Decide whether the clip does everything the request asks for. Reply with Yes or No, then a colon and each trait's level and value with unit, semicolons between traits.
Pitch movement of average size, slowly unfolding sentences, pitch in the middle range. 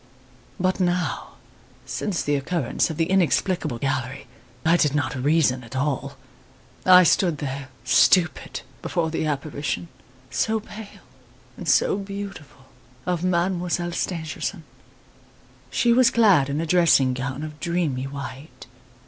Yes: average, 4.6 semitones; slow, 125 wpm; medium, 160 Hz